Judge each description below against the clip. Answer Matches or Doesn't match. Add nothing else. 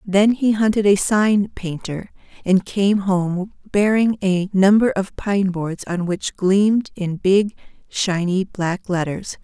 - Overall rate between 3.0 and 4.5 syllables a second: Matches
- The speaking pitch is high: Matches